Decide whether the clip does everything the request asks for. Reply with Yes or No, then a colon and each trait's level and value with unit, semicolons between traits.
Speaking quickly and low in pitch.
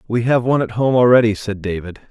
Yes: fast, 230 wpm; low, 115 Hz